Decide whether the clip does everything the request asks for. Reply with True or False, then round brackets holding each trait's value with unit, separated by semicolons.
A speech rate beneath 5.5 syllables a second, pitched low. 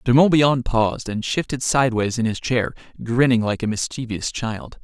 True (5.2 syllables/s; 120 Hz)